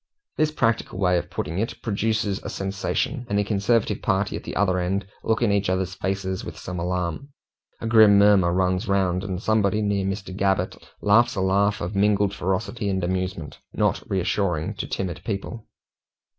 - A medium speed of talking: Yes, average, 175 wpm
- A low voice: Yes, low, 100 Hz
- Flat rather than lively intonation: Yes, narrow, 2.0 semitones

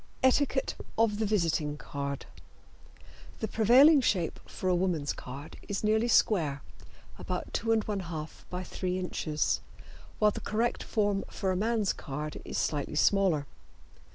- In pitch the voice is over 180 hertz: Yes, high, 190 Hz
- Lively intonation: Yes, wide, 6.0 semitones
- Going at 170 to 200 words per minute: No, slow, 135 wpm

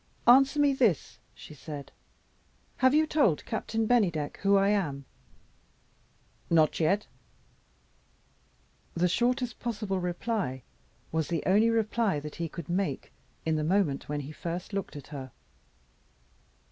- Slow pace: Yes, slow, 130 wpm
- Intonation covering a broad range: Yes, wide, 6.6 semitones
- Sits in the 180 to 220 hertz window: Yes, medium, 185 Hz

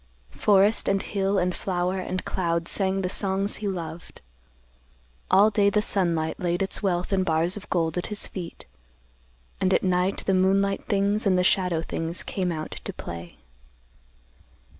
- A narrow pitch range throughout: Yes, narrow, 2.2 semitones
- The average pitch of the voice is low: No, medium, 185 Hz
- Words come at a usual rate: Yes, average, 160 wpm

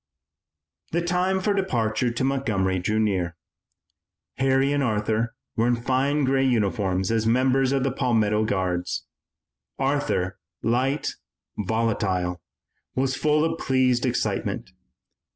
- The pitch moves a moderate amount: Yes, average, 4.2 semitones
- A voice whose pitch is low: Yes, low, 120 Hz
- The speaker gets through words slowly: Yes, slow, 115 wpm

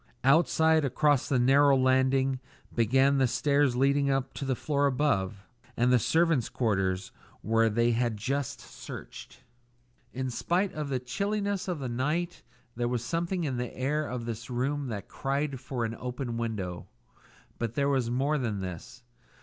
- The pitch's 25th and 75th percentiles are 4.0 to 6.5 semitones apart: No, average, 3.3 semitones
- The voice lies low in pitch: Yes, low, 130 Hz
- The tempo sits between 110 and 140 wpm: No, average, 160 wpm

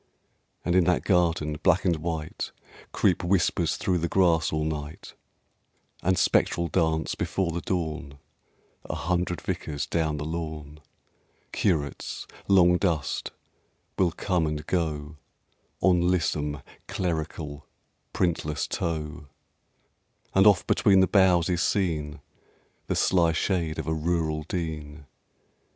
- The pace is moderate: No, slow, 120 wpm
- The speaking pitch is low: Yes, very low, 80 Hz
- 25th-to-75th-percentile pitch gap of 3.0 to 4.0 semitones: No, narrow, 2.6 semitones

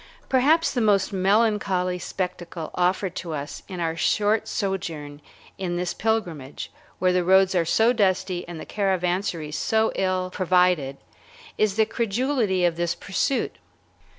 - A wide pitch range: No, average, 3.0 semitones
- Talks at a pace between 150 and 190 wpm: No, average, 140 wpm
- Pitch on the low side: No, medium, 185 Hz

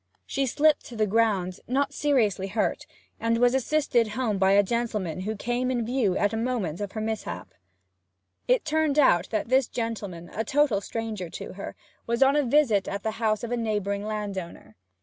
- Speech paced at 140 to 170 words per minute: No, average, 190 wpm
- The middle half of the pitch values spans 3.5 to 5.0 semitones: Yes, average, 3.9 semitones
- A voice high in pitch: Yes, high, 225 Hz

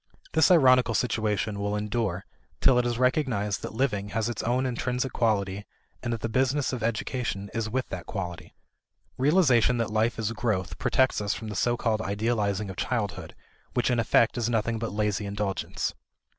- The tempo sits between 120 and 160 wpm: No, average, 175 wpm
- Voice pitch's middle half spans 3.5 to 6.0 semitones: No, average, 3.1 semitones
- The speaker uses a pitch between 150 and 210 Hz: No, low, 115 Hz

